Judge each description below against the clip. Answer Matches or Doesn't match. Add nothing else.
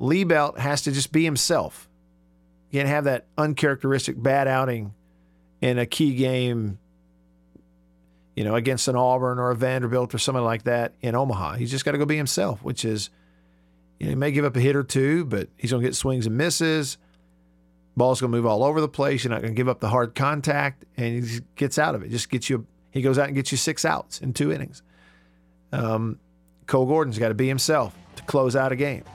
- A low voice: Matches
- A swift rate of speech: Matches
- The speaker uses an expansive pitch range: Matches